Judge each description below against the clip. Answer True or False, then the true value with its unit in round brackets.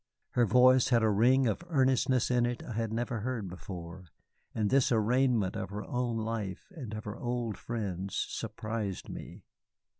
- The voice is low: True (115 Hz)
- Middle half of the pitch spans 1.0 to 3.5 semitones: True (3.0 semitones)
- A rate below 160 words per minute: False (170 wpm)